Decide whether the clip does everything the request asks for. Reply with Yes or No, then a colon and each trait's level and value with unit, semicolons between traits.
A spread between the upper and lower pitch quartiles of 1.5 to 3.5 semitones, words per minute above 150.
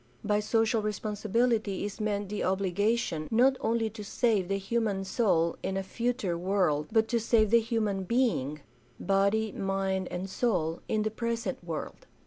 Yes: average, 2.8 semitones; average, 165 wpm